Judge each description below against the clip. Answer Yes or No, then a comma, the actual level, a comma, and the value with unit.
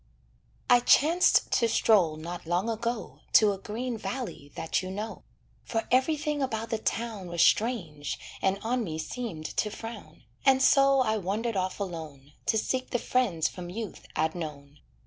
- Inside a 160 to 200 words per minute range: Yes, average, 165 wpm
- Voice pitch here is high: Yes, high, 215 Hz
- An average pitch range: No, wide, 6.0 semitones